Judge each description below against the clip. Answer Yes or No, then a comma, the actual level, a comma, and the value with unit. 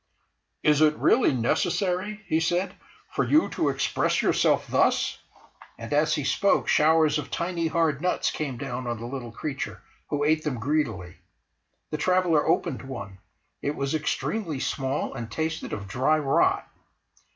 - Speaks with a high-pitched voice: No, medium, 150 Hz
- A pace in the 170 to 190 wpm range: No, average, 150 wpm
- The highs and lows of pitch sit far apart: No, average, 4.0 semitones